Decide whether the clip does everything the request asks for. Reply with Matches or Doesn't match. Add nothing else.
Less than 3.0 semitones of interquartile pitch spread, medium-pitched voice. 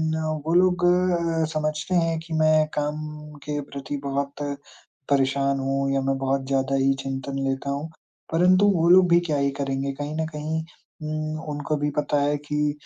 Matches